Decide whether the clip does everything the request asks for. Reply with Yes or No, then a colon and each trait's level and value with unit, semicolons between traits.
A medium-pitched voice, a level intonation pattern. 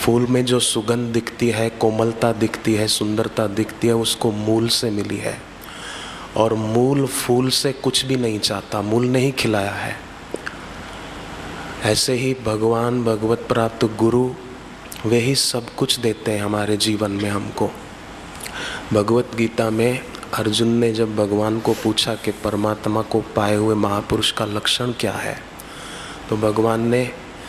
No: low, 115 Hz; narrow, 1.9 semitones